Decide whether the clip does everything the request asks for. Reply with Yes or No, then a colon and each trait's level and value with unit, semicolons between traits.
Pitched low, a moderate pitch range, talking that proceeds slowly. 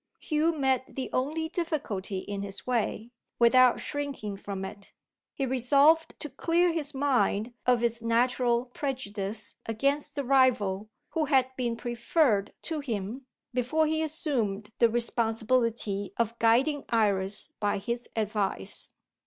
No: high, 240 Hz; average, 4.6 semitones; slow, 130 wpm